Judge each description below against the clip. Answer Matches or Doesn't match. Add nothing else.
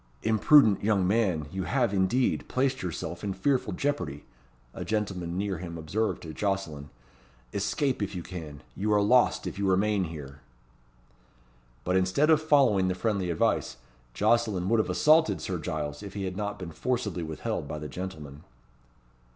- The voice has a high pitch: Doesn't match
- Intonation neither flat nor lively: Matches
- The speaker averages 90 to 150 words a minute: Doesn't match